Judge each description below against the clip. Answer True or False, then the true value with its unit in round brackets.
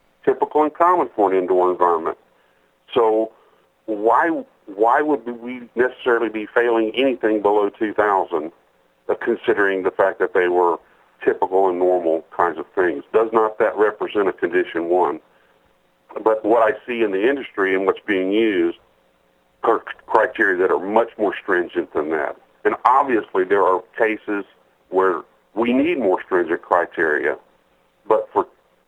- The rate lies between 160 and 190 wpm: False (145 wpm)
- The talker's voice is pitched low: True (110 Hz)